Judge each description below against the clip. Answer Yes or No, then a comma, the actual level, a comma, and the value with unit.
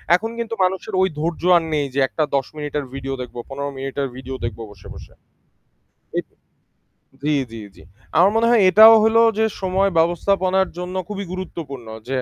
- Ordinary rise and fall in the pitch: No, wide, 6.0 semitones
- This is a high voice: No, medium, 170 Hz